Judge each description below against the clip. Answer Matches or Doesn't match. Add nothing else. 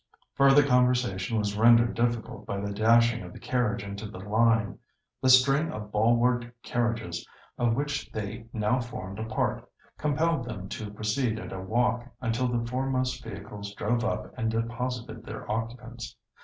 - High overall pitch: Doesn't match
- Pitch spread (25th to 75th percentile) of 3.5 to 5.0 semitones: Doesn't match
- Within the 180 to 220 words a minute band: Doesn't match